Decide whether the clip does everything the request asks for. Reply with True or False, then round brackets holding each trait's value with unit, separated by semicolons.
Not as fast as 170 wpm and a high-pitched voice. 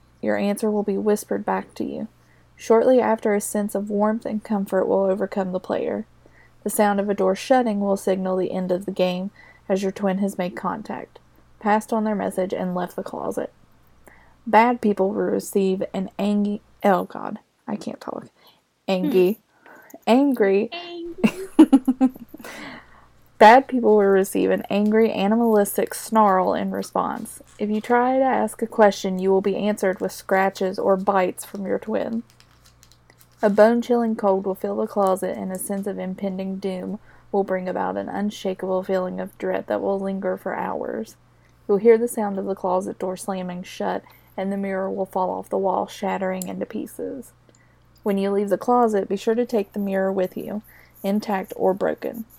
False (175 wpm; 200 Hz)